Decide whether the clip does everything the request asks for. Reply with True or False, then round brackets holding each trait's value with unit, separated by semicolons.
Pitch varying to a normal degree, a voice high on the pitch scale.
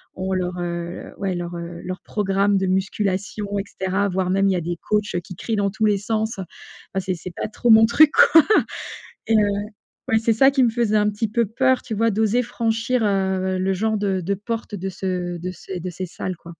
True (3.0 semitones; 200 Hz)